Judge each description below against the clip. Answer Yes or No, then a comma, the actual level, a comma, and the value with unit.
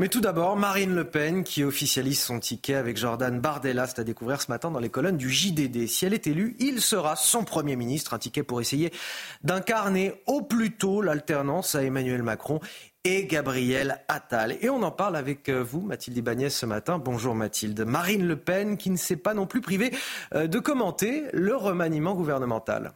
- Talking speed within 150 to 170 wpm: No, average, 195 wpm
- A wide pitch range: Yes, wide, 7.2 semitones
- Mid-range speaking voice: Yes, medium, 155 Hz